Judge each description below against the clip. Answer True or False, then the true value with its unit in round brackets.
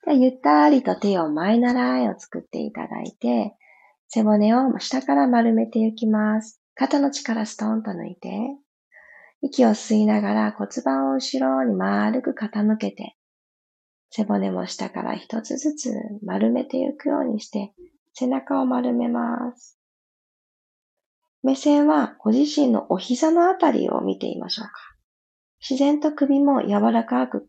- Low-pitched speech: False (230 Hz)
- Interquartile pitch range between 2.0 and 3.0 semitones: False (5.2 semitones)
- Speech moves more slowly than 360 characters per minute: True (265 characters per minute)